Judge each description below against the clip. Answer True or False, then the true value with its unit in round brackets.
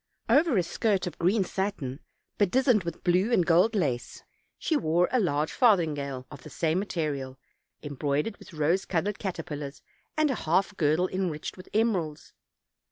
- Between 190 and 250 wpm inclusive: False (155 wpm)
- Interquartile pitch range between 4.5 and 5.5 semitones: True (5.2 semitones)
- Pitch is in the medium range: True (175 Hz)